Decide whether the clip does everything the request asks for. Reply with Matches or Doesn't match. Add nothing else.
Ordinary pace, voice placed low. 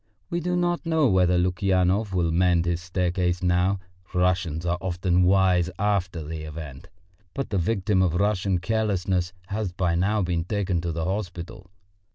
Matches